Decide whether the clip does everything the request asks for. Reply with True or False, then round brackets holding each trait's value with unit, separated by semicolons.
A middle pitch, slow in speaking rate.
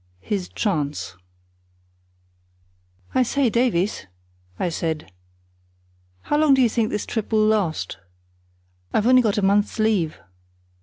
False (210 Hz; 120 wpm)